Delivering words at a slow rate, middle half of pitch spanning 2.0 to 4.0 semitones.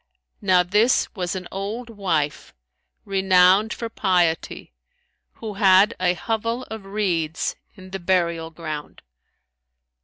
Yes: slow, 115 wpm; average, 3.2 semitones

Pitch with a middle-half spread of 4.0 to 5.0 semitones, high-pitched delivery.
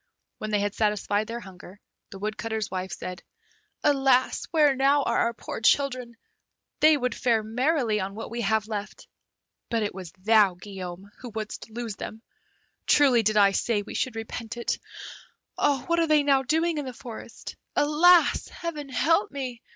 Yes: average, 4.7 semitones; high, 230 Hz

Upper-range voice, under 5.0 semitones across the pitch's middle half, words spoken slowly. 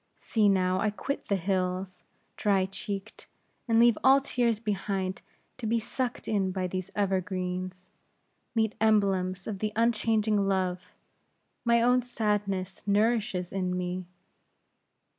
Yes: high, 200 Hz; average, 3.1 semitones; slow, 125 wpm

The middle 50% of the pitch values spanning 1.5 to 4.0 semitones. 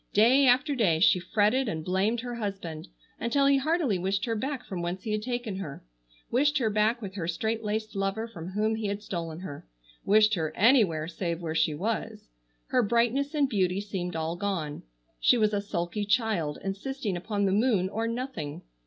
No: average, 4.6 semitones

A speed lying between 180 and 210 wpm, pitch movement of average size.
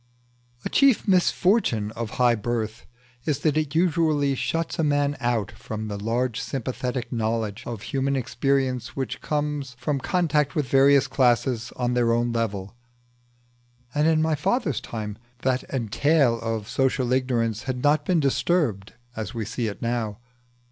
No: average, 150 wpm; average, 4.1 semitones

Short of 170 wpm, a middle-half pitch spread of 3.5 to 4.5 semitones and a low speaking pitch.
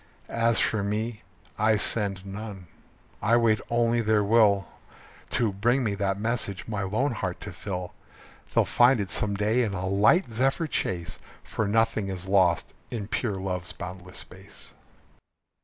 No: average, 155 wpm; average, 2.9 semitones; low, 105 Hz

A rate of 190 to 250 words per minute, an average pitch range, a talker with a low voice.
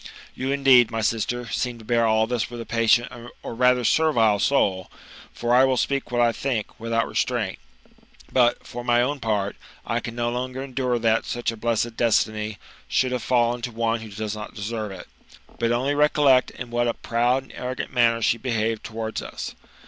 No: average, 195 wpm; narrow, 1.9 semitones; low, 120 Hz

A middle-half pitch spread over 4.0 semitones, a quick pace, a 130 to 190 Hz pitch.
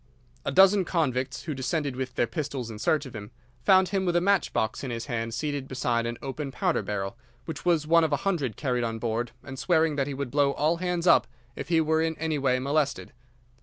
Yes: average, 4.5 semitones; fast, 230 wpm; medium, 140 Hz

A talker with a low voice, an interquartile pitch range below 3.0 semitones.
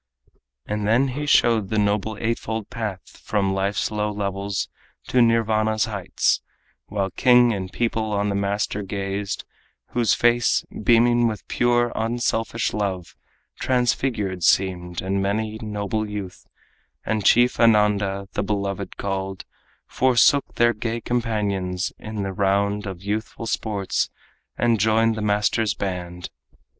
Yes: low, 105 Hz; narrow, 2.6 semitones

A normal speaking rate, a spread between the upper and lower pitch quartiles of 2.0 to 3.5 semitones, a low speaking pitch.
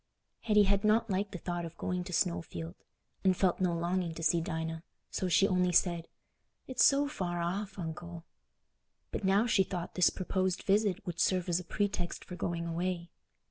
No: average, 180 wpm; narrow, 2.4 semitones; medium, 180 Hz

